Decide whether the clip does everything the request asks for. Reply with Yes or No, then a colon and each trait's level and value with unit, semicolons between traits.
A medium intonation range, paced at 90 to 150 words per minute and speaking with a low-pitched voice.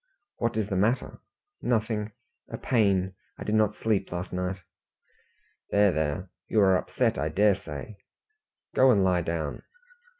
Yes: average, 3.1 semitones; average, 145 wpm; low, 100 Hz